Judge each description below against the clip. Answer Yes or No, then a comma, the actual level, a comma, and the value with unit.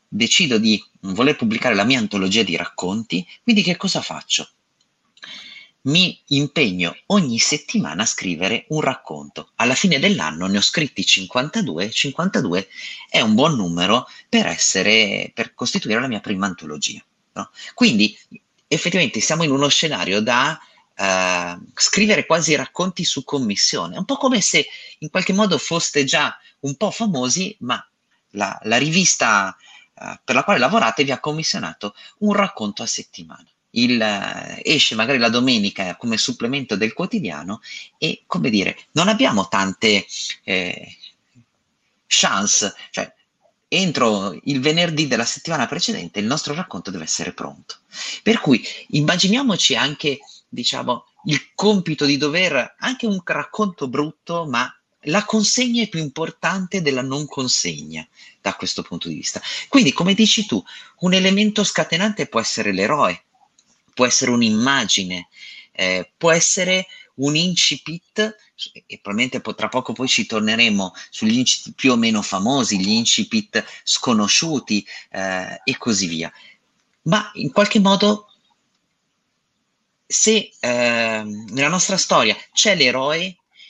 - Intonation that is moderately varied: No, wide, 9.0 semitones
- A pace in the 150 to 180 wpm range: No, average, 135 wpm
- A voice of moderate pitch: Yes, medium, 165 Hz